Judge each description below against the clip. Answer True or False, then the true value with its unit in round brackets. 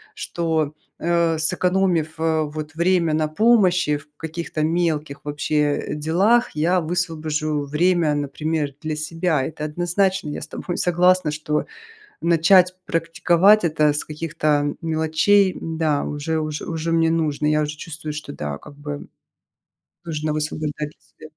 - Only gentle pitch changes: True (2.2 semitones)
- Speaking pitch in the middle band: True (160 Hz)